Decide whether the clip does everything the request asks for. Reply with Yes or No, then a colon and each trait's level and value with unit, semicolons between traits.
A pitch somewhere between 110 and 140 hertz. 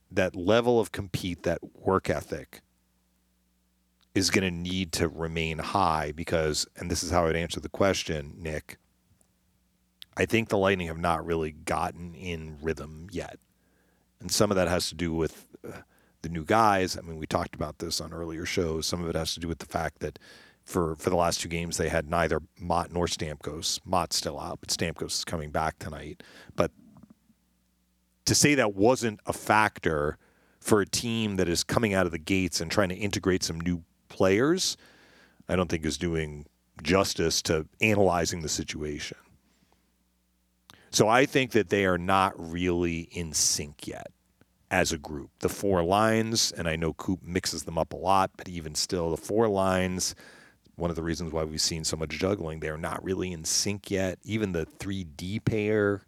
No: very low, 85 Hz